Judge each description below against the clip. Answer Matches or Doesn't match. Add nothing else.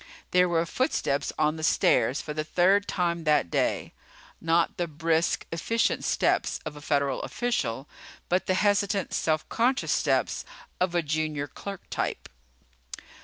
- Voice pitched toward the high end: Doesn't match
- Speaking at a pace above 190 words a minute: Doesn't match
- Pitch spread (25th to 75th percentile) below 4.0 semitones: Matches